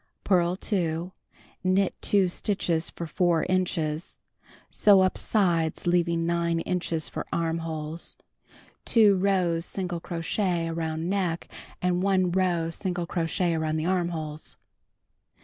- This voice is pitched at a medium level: Yes, medium, 175 Hz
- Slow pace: Yes, slow, 115 wpm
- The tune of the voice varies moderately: No, narrow, 2.0 semitones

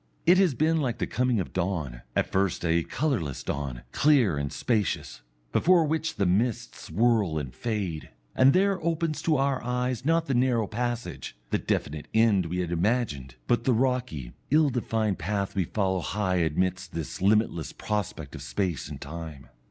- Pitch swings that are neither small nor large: No, wide, 7.1 semitones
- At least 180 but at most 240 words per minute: No, average, 170 wpm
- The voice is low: Yes, low, 105 Hz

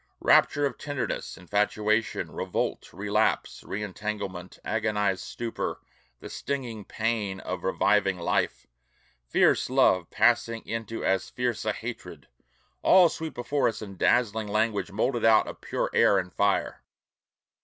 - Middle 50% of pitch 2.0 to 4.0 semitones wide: Yes, average, 2.9 semitones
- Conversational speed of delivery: No, slow, 130 wpm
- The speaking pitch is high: No, low, 105 Hz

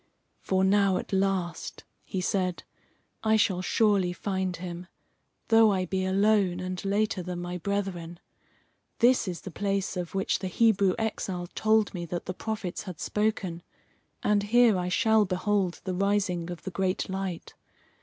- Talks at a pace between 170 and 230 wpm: No, average, 155 wpm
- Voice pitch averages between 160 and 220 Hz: Yes, high, 190 Hz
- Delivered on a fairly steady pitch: Yes, narrow, 2.3 semitones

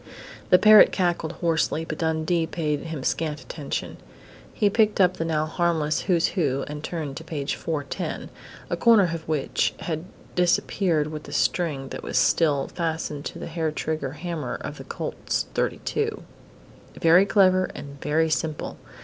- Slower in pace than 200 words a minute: Yes, average, 160 wpm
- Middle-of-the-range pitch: Yes, medium, 160 Hz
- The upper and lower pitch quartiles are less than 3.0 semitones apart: Yes, narrow, 2.4 semitones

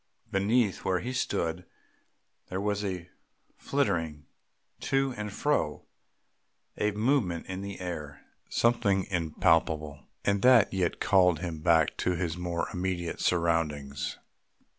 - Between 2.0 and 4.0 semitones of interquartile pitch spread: Yes, average, 3.7 semitones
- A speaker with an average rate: No, slow, 120 wpm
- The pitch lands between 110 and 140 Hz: No, very low, 90 Hz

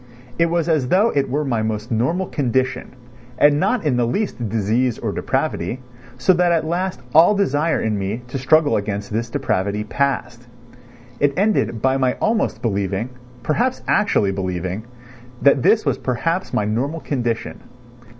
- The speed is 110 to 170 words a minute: Yes, average, 160 wpm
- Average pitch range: No, wide, 6.5 semitones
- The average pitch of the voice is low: Yes, low, 130 Hz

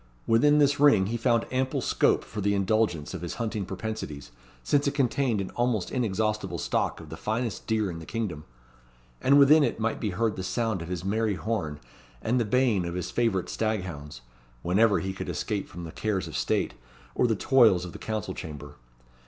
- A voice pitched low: Yes, low, 110 Hz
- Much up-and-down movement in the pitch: No, average, 4.2 semitones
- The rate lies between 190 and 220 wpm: Yes, average, 200 wpm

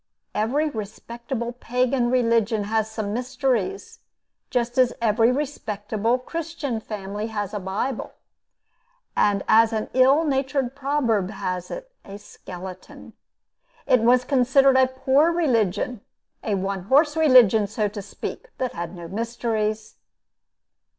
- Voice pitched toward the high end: Yes, high, 235 Hz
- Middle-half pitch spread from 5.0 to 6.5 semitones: No, average, 4.1 semitones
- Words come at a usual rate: No, slow, 125 wpm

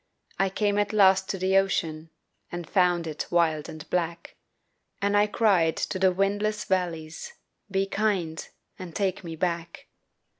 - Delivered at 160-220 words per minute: No, average, 150 wpm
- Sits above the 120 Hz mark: Yes, medium, 185 Hz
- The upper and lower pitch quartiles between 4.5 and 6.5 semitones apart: No, average, 2.9 semitones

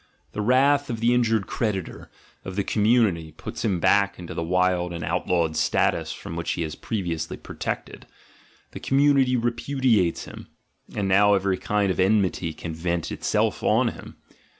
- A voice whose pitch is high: No, very low, 95 Hz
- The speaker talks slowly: No, average, 165 wpm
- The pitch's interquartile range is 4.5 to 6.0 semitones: Yes, average, 5.0 semitones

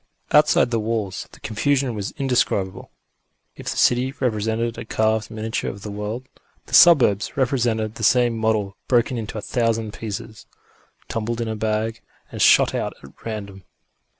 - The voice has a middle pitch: No, low, 110 Hz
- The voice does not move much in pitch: Yes, narrow, 2.0 semitones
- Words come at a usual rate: Yes, average, 155 wpm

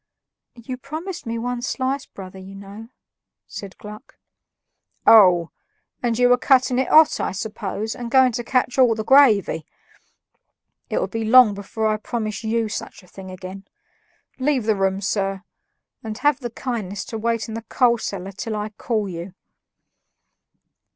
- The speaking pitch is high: Yes, high, 220 Hz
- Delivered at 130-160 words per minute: Yes, average, 155 wpm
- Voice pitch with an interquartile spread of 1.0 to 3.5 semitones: No, average, 3.9 semitones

